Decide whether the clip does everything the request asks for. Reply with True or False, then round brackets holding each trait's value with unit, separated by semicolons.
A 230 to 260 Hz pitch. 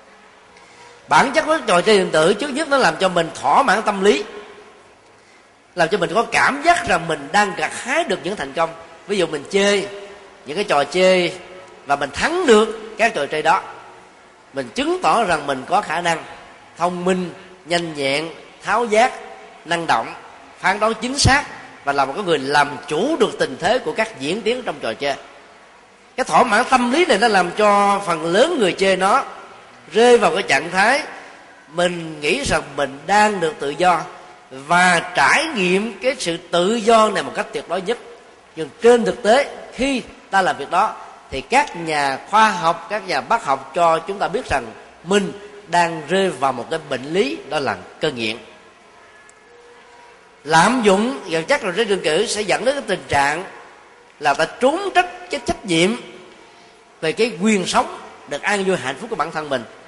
False (190 Hz)